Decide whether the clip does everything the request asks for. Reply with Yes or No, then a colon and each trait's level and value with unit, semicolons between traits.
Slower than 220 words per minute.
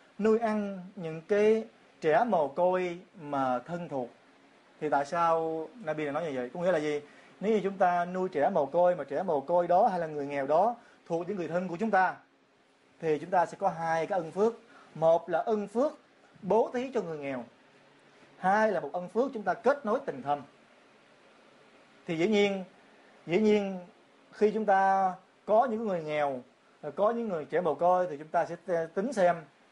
Yes: average, 200 wpm